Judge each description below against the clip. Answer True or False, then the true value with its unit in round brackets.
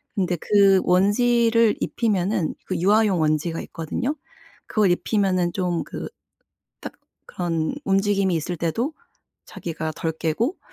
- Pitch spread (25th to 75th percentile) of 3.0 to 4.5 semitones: True (4.1 semitones)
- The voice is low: False (190 Hz)